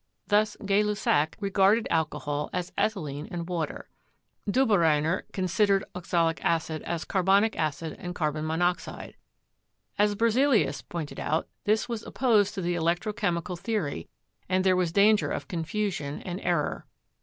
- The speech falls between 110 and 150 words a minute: Yes, average, 145 wpm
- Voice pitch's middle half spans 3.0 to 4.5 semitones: Yes, average, 4.2 semitones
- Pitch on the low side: No, medium, 180 Hz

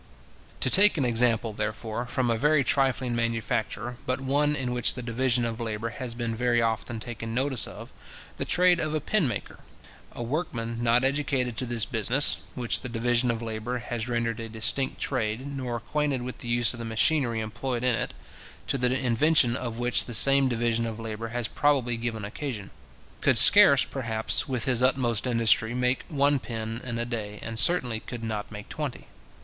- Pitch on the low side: Yes, low, 120 Hz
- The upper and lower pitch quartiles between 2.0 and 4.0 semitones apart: Yes, narrow, 2.5 semitones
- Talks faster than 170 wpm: Yes, average, 190 wpm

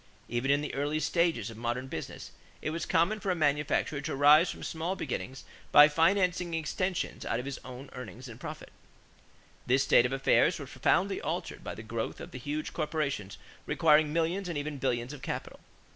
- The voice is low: No, medium, 145 Hz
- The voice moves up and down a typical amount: Yes, average, 4.2 semitones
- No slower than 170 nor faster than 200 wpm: Yes, average, 190 wpm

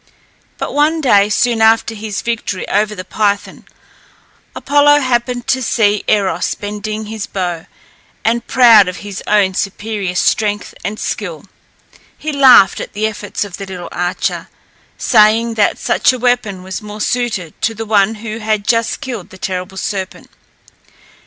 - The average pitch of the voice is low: No, high, 215 Hz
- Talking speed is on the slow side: No, average, 150 wpm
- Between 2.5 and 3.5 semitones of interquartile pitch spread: Yes, average, 2.8 semitones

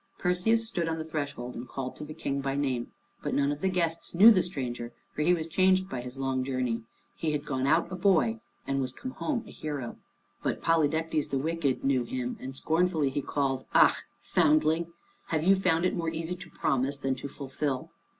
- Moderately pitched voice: Yes, medium, 150 Hz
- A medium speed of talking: No, fast, 210 wpm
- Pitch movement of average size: Yes, average, 4.1 semitones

